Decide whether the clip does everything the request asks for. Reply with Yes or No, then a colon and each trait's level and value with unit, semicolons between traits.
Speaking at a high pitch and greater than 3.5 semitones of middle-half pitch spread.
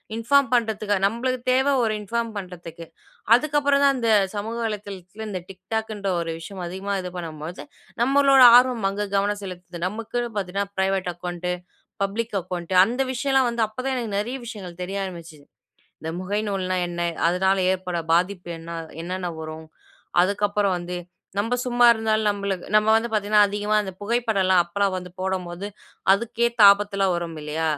Yes: high, 200 Hz; average, 3.9 semitones